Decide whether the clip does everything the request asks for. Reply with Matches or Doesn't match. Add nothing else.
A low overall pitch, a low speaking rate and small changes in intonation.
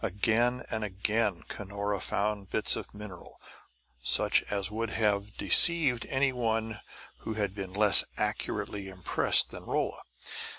Matches